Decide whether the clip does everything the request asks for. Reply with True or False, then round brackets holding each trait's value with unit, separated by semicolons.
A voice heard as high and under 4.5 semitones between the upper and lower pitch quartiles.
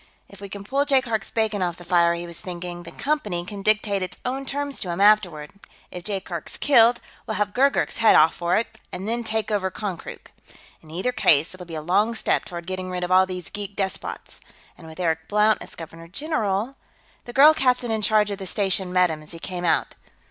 True (195 Hz; 3.9 semitones)